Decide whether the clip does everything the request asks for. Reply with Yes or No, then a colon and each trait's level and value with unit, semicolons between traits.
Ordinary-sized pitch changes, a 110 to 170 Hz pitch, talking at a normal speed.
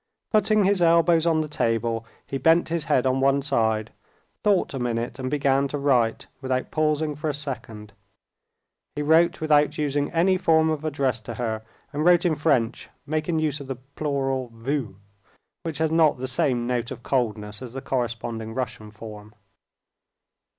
Yes: average, 4.7 semitones; medium, 140 Hz; average, 170 wpm